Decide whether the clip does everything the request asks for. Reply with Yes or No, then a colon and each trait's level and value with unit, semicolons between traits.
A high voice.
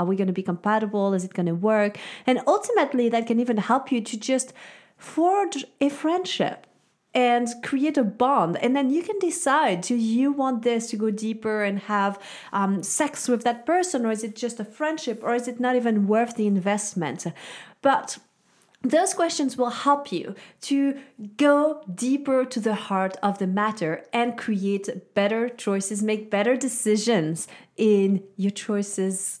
Yes: high, 230 Hz